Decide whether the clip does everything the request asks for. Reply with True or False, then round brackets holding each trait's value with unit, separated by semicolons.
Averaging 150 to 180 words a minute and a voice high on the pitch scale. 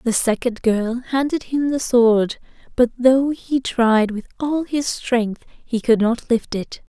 True (175 wpm; 245 Hz)